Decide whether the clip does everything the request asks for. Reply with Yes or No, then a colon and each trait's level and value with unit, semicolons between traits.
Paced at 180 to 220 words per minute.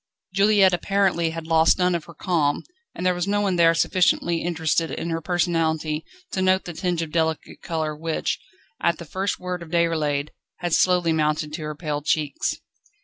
Yes: average, 185 wpm